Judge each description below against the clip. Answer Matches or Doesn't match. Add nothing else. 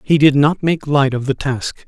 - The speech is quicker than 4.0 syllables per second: Matches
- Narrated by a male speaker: Matches